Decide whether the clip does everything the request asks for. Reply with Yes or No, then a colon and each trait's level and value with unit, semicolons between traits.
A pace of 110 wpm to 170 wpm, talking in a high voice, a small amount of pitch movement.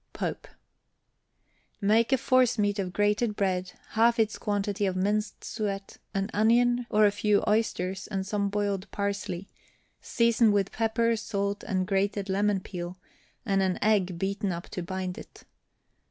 Yes: average, 145 wpm; high, 205 Hz; narrow, 2.1 semitones